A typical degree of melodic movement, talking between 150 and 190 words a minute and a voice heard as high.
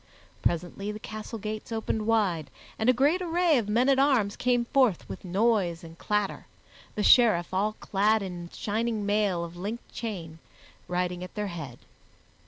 Yes: average, 4.4 semitones; average, 165 wpm; high, 210 Hz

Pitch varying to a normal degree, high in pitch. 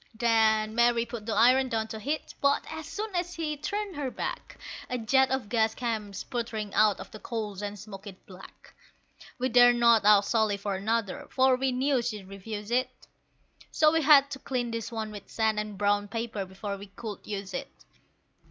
Yes: average, 3.7 semitones; high, 225 Hz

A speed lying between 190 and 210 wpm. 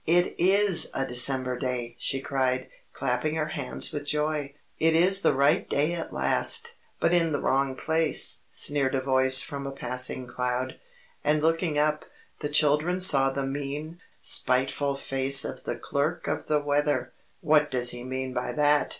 No: average, 165 wpm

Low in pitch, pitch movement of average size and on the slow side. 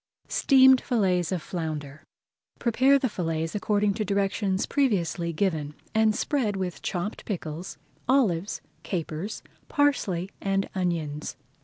No: high, 190 Hz; average, 4.5 semitones; slow, 115 wpm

